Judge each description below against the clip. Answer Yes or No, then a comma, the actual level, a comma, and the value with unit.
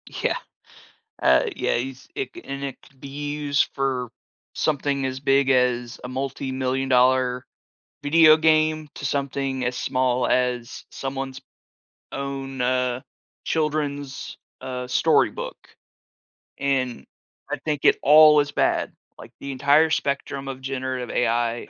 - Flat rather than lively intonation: Yes, narrow, 1.9 semitones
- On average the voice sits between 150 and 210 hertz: No, low, 135 Hz